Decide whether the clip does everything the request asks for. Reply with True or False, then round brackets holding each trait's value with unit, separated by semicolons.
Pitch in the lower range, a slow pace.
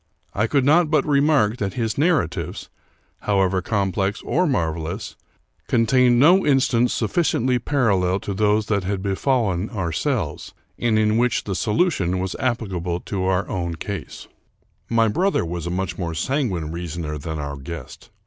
False (100 Hz; 150 wpm)